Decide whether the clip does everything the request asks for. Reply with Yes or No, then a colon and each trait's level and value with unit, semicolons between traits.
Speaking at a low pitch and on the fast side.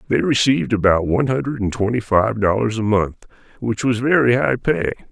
No: low, 115 Hz; average, 190 wpm